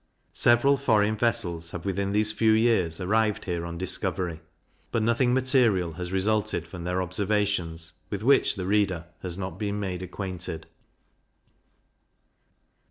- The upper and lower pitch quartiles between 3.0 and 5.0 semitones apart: Yes, average, 3.6 semitones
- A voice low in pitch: Yes, low, 100 Hz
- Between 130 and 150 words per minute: Yes, slow, 135 wpm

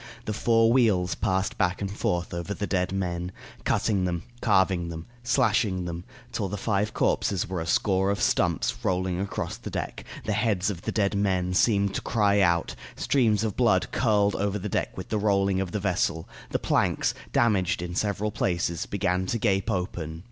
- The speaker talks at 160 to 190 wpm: Yes, average, 185 wpm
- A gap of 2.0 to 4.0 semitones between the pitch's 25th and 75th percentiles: Yes, narrow, 2.5 semitones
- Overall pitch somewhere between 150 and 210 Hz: No, very low, 95 Hz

